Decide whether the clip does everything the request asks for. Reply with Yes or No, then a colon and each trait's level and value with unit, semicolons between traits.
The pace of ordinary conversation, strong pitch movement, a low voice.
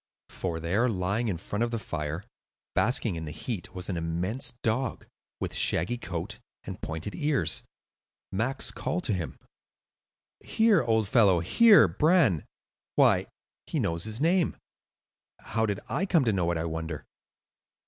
Yes: average, 150 wpm; wide, 6.7 semitones; low, 105 Hz